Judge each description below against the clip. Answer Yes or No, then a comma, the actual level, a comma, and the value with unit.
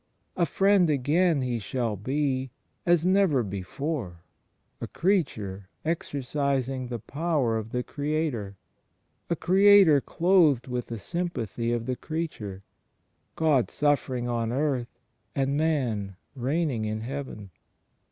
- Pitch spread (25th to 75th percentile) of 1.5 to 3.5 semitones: No, wide, 5.4 semitones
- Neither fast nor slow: No, slow, 115 wpm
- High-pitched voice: No, low, 135 Hz